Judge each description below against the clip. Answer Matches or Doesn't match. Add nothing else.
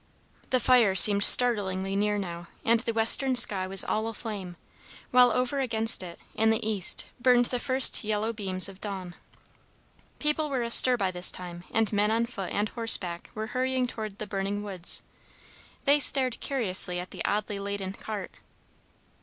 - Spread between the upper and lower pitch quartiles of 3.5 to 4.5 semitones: Matches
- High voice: Matches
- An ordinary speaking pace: Matches